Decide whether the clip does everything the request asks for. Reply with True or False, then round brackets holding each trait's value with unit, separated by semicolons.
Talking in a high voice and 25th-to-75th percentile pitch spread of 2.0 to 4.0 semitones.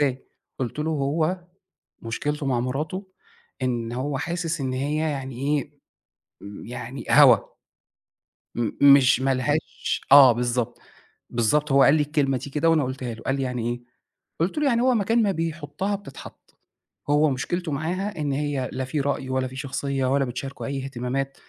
False (140 Hz; 3.1 semitones)